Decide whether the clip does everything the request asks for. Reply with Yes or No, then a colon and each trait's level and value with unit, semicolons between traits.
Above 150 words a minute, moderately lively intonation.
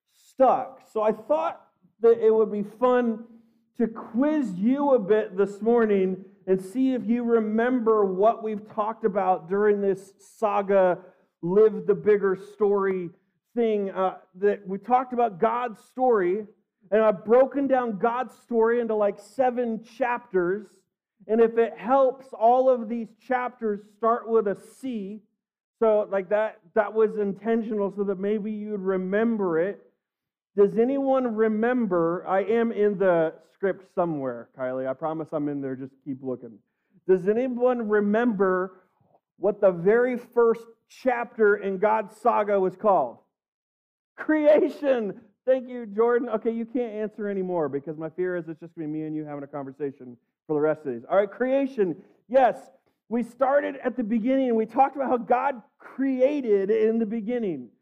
Yes: average, 160 wpm; average, 3.5 semitones